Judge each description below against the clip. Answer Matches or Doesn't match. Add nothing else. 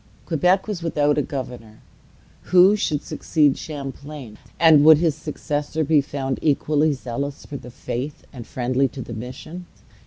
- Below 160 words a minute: Matches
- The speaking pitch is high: Doesn't match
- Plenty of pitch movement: Doesn't match